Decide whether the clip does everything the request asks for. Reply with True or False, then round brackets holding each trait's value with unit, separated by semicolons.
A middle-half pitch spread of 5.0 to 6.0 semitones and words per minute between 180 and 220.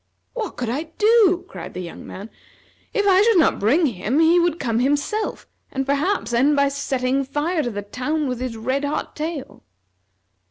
True (5.4 semitones; 185 wpm)